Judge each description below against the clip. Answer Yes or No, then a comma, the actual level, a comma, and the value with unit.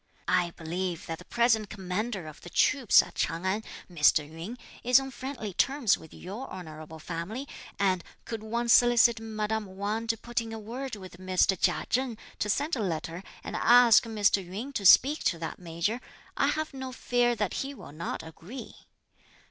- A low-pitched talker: No, high, 215 Hz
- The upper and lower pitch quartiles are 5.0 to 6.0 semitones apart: Yes, average, 5.3 semitones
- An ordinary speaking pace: Yes, average, 180 wpm